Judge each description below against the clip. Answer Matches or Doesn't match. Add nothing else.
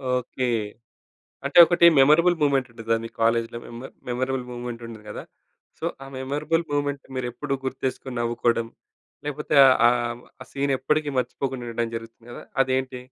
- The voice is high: Doesn't match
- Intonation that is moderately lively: Matches